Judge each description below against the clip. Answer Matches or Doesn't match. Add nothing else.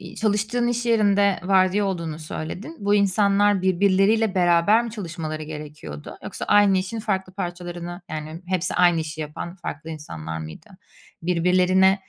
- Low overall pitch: Doesn't match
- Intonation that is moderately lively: Matches